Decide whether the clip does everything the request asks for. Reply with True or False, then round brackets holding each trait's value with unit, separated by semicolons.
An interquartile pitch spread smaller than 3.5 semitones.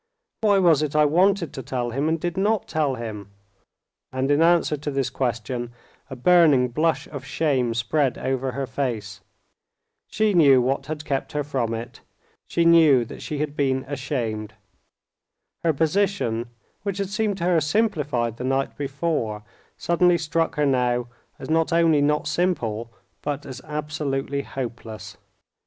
False (4.7 semitones)